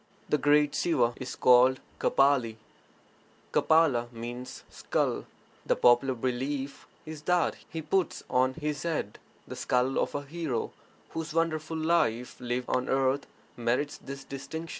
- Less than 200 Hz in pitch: Yes, low, 135 Hz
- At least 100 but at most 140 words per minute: Yes, slow, 135 wpm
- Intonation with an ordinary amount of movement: Yes, average, 3.9 semitones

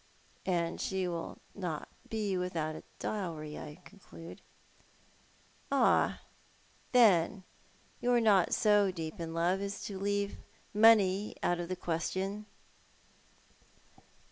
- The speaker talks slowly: Yes, slow, 120 wpm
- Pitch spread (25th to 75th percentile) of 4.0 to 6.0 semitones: No, average, 3.3 semitones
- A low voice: No, high, 190 Hz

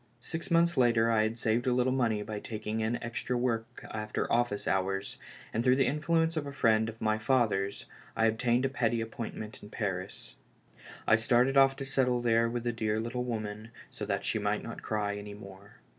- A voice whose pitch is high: No, low, 115 Hz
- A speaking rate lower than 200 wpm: No, fast, 205 wpm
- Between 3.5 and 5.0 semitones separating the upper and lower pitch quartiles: No, narrow, 2.6 semitones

